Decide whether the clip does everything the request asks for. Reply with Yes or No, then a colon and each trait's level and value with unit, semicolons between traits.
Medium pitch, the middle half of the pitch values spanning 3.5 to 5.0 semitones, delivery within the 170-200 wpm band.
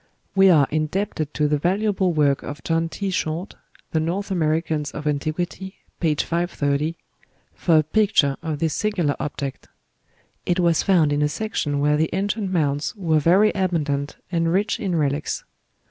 No: medium, 165 Hz; average, 4.0 semitones; average, 160 wpm